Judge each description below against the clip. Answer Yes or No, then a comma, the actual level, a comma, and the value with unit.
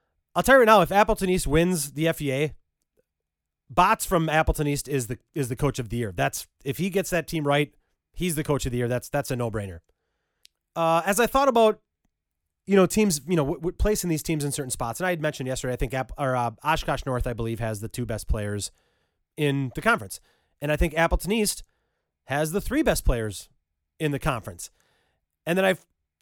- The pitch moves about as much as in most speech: No, wide, 6.4 semitones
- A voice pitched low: No, medium, 145 Hz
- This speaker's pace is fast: Yes, fast, 225 wpm